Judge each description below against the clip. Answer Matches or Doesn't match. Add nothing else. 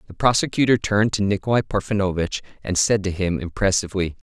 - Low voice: Matches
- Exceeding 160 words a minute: Doesn't match